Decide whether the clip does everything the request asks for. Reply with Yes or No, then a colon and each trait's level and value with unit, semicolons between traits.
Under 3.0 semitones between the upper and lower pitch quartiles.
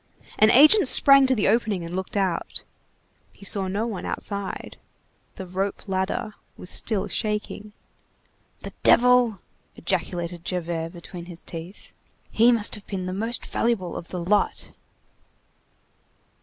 No: average, 3.6 semitones